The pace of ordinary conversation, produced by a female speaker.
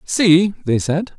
No: average, 150 wpm; male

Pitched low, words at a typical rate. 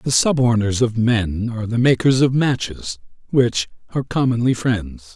Yes: low, 115 Hz; average, 150 wpm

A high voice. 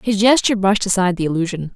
Yes: high, 195 Hz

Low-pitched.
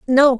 No: very high, 265 Hz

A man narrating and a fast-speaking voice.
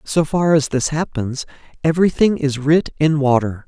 No: male; average, 165 wpm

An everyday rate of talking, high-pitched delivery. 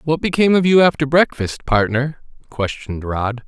No: average, 155 wpm; medium, 140 Hz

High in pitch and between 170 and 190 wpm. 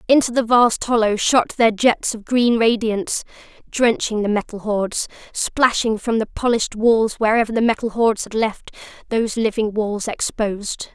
No: high, 225 Hz; average, 160 wpm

